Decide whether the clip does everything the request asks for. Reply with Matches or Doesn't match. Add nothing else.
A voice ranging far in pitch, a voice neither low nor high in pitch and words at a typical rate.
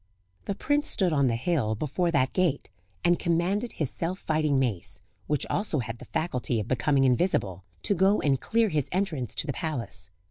Matches